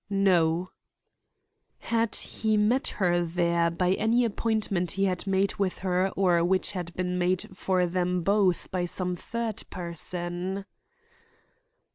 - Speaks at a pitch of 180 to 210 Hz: Yes, medium, 185 Hz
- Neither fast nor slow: No, slow, 130 wpm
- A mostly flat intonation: Yes, narrow, 2.1 semitones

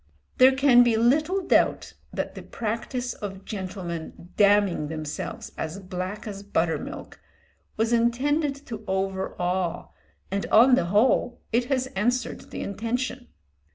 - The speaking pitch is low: No, high, 215 Hz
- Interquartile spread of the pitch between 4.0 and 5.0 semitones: Yes, average, 4.6 semitones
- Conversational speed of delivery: No, slow, 130 wpm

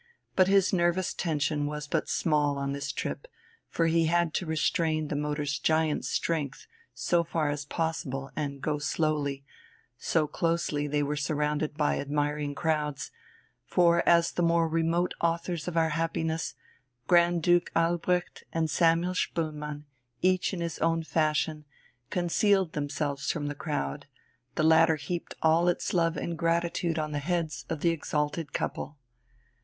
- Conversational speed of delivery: Yes, average, 150 wpm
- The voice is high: No, medium, 160 Hz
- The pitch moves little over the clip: Yes, narrow, 2.3 semitones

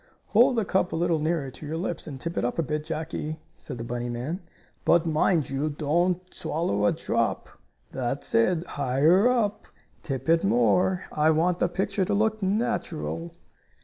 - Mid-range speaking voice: Yes, medium, 165 Hz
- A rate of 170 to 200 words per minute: Yes, average, 180 wpm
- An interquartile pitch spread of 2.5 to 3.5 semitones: No, average, 4.0 semitones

